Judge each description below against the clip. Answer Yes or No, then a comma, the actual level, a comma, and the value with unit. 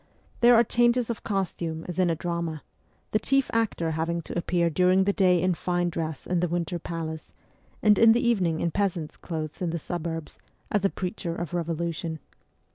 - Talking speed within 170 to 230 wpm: Yes, average, 190 wpm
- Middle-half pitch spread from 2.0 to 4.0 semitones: Yes, average, 3.0 semitones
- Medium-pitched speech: Yes, medium, 175 Hz